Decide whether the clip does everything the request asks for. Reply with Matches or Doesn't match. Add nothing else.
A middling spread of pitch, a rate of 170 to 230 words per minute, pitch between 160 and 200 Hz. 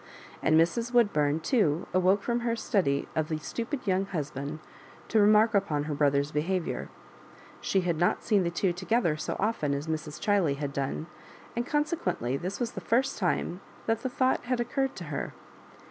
Doesn't match